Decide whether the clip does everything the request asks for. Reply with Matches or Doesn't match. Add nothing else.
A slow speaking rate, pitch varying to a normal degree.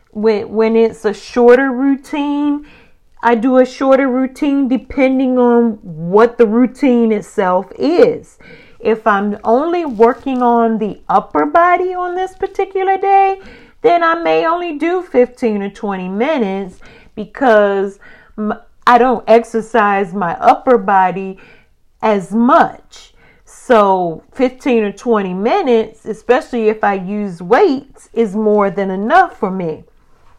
Matches